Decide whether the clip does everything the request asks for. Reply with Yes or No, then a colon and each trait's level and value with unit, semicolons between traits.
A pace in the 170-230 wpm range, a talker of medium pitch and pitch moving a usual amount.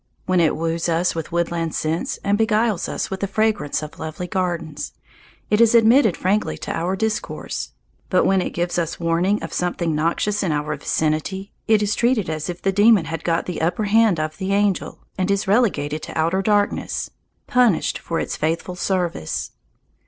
Yes: average, 180 wpm; medium, 180 Hz; average, 4.0 semitones